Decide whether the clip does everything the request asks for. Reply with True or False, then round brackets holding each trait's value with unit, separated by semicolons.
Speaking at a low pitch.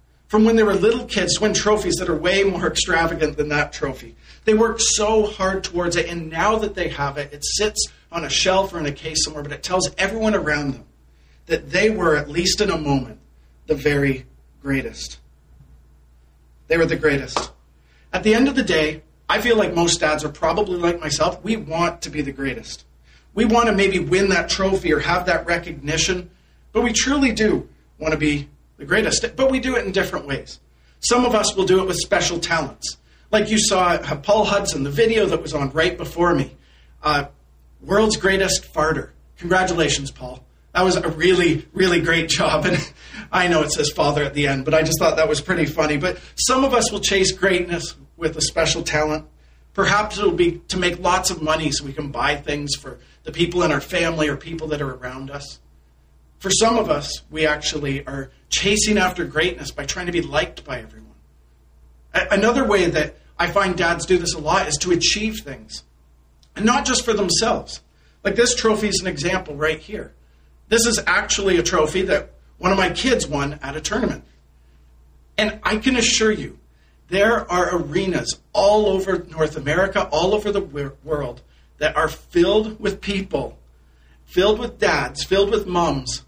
False (170 Hz)